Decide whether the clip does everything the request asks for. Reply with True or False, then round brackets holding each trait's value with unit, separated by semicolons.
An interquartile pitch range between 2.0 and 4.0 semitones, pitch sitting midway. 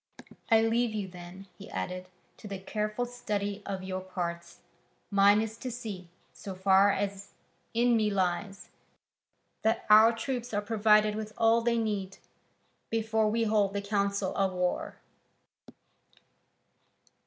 False (2.5 semitones; 205 Hz)